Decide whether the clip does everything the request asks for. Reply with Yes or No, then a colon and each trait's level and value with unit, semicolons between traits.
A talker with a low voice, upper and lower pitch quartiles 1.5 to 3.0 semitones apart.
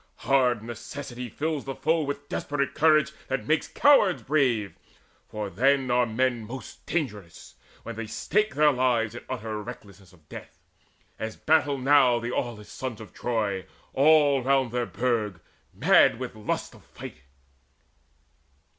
No: low, 125 Hz; average, 4.2 semitones